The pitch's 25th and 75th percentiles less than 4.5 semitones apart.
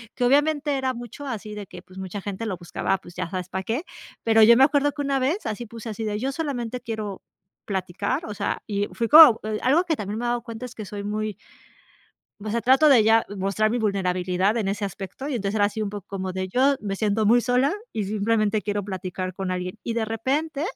Yes: average, 4.1 semitones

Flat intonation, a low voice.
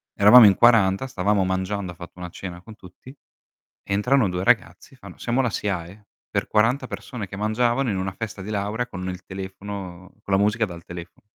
No: average, 3.0 semitones; low, 100 Hz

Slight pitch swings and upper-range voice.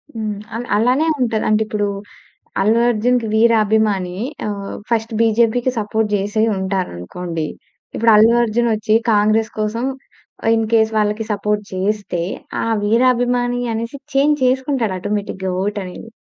Yes: narrow, 2.1 semitones; high, 220 Hz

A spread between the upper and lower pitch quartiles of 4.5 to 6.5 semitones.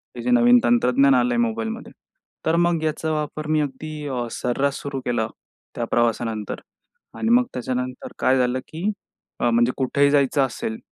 Yes: wide, 5.6 semitones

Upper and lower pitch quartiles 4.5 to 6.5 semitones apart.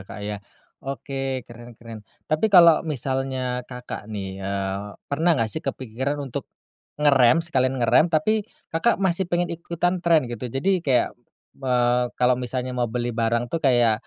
Yes: average, 5.0 semitones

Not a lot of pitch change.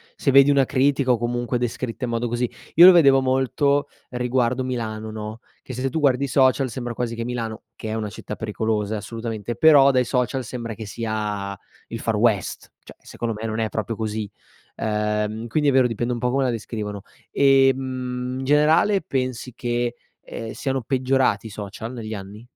No: average, 3.2 semitones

